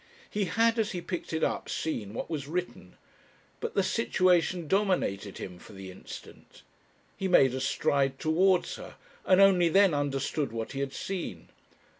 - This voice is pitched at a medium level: Yes, medium, 160 Hz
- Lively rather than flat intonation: Yes, wide, 5.7 semitones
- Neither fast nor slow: Yes, average, 165 wpm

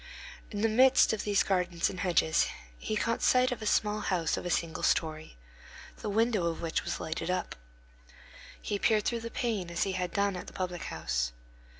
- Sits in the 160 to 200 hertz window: Yes, high, 190 Hz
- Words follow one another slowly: No, average, 200 wpm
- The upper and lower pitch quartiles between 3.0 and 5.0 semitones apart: Yes, average, 4.1 semitones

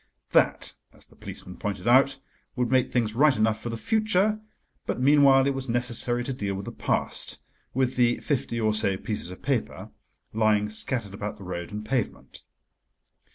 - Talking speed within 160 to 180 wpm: Yes, average, 170 wpm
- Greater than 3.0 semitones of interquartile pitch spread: Yes, average, 4.0 semitones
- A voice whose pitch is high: No, low, 120 Hz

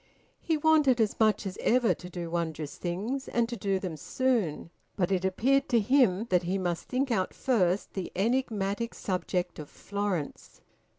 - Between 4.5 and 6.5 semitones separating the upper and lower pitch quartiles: Yes, average, 5.1 semitones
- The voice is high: Yes, high, 200 Hz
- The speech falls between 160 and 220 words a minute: Yes, average, 170 wpm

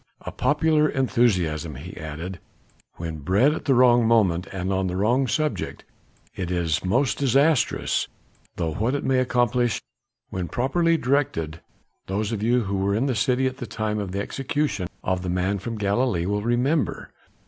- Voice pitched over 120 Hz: No, low, 110 Hz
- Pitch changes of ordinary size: No, wide, 6.0 semitones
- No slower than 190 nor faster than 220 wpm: No, average, 165 wpm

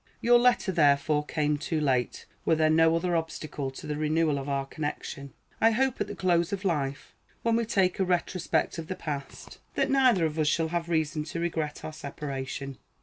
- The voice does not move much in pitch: No, average, 3.3 semitones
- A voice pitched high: No, medium, 160 Hz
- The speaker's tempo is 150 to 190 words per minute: No, average, 200 wpm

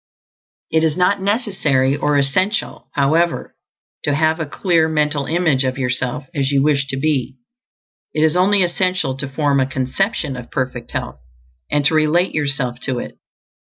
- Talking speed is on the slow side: No, average, 160 wpm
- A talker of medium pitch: Yes, medium, 150 Hz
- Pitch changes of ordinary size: Yes, average, 3.9 semitones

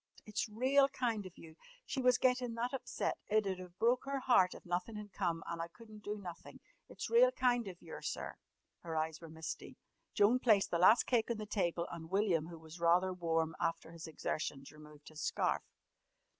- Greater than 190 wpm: Yes, average, 200 wpm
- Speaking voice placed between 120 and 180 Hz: No, high, 190 Hz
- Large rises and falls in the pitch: Yes, wide, 5.7 semitones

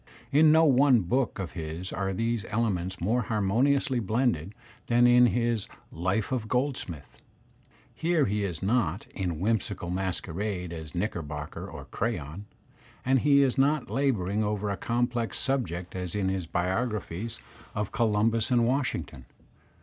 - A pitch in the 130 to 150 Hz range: No, low, 105 Hz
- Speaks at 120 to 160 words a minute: Yes, average, 150 wpm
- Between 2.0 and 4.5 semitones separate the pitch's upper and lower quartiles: No, average, 5.1 semitones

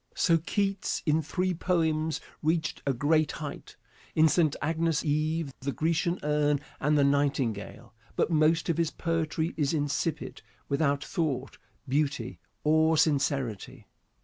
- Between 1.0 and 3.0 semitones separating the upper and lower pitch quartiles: Yes, narrow, 2.4 semitones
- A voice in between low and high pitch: Yes, medium, 155 Hz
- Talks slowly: Yes, slow, 130 wpm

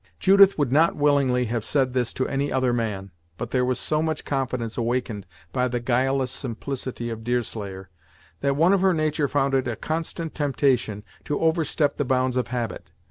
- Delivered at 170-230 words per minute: Yes, average, 185 wpm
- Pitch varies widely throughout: No, average, 3.2 semitones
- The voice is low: Yes, low, 130 Hz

